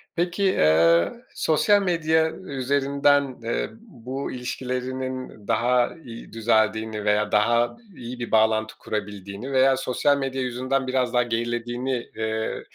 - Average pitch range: Yes, average, 3.5 semitones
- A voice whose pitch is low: Yes, low, 125 Hz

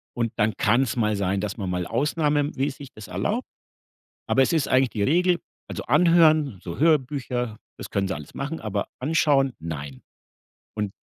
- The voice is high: No, low, 125 Hz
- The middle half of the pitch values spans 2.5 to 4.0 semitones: No, wide, 6.6 semitones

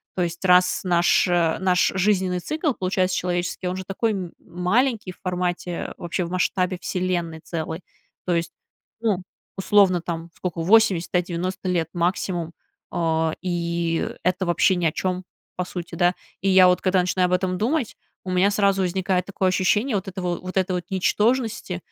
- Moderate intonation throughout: No, narrow, 1.5 semitones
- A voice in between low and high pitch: Yes, medium, 180 Hz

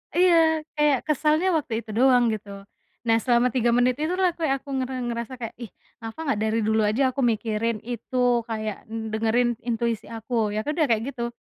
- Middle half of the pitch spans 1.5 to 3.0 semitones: No, average, 3.8 semitones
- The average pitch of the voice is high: Yes, high, 240 Hz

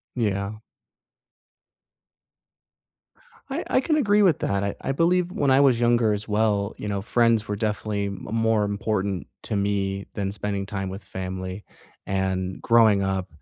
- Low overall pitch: Yes, low, 105 Hz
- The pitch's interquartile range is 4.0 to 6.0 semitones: No, average, 2.9 semitones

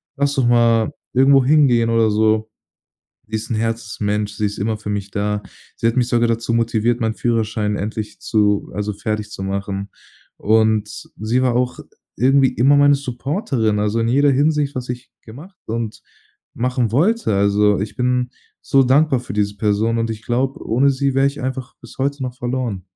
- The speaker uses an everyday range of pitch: Yes, average, 3.5 semitones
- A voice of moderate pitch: No, low, 115 Hz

